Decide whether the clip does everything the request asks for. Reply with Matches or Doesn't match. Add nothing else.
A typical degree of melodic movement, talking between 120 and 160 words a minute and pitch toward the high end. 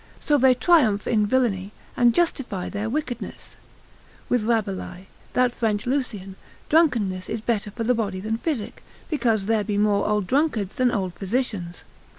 Matches